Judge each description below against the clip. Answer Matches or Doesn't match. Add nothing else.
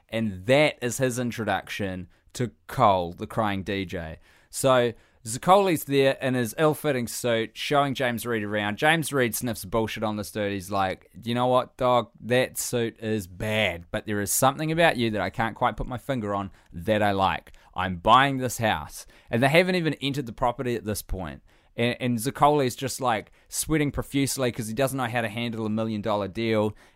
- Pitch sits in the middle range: Doesn't match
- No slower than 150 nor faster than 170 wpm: Doesn't match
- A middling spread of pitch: Matches